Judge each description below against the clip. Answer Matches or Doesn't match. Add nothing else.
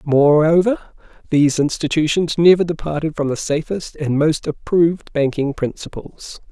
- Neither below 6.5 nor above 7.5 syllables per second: Doesn't match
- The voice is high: Doesn't match